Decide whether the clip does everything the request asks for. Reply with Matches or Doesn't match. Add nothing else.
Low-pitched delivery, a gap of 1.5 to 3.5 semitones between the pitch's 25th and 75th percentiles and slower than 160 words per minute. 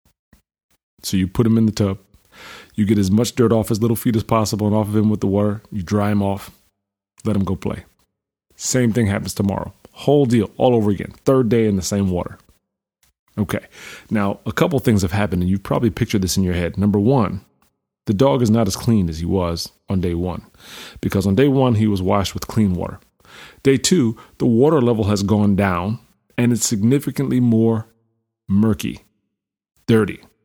Doesn't match